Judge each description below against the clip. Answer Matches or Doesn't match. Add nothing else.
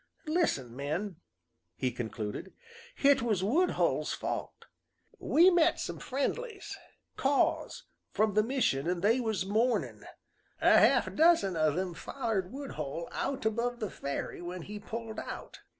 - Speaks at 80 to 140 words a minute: Matches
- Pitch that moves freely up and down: Matches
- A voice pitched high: Matches